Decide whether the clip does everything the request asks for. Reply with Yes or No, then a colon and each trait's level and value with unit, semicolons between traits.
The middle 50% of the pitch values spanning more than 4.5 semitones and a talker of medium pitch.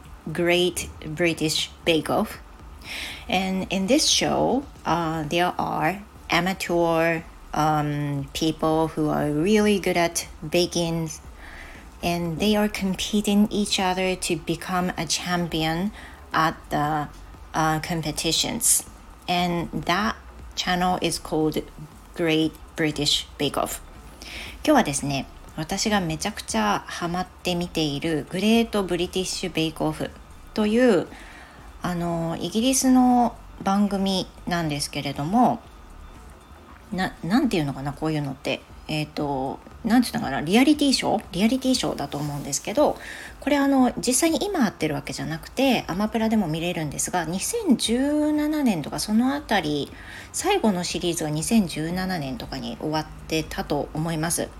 Yes: average, 5.2 semitones; medium, 170 Hz